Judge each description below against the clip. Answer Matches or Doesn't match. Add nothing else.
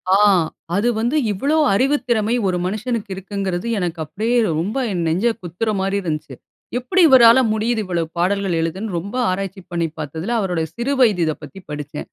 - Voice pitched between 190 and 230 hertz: Matches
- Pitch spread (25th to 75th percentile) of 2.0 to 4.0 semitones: Doesn't match